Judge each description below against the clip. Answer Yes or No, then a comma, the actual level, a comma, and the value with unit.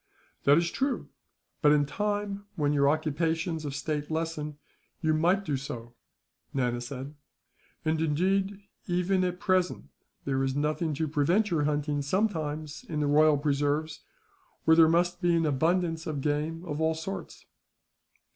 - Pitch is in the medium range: Yes, medium, 155 Hz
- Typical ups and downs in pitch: Yes, average, 3.1 semitones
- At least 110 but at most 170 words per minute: Yes, average, 150 wpm